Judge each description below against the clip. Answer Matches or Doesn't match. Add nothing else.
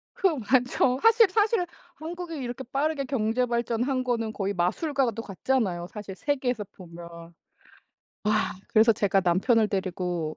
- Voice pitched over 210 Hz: Matches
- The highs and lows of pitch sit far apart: Matches